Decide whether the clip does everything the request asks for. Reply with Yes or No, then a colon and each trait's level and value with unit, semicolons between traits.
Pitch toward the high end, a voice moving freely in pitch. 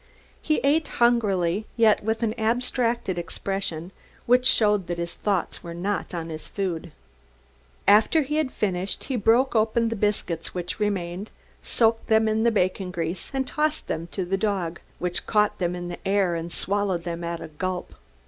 No: high, 200 Hz; average, 4.4 semitones